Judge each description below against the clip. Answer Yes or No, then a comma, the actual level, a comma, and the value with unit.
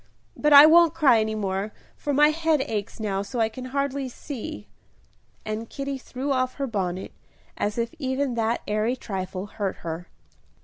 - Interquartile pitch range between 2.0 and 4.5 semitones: No, average, 5.1 semitones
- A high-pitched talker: Yes, high, 235 Hz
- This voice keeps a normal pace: Yes, average, 170 wpm